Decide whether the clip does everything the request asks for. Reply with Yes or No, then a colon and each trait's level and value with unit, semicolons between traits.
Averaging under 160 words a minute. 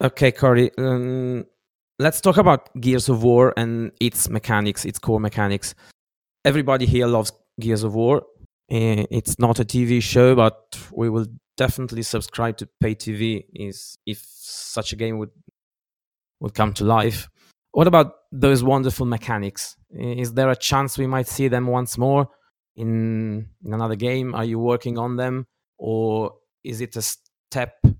Yes: average, 150 wpm